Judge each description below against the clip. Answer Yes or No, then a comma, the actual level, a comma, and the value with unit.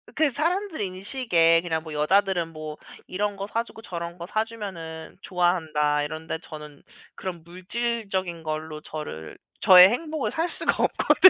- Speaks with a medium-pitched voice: Yes, medium, 175 Hz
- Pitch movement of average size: Yes, average, 4.9 semitones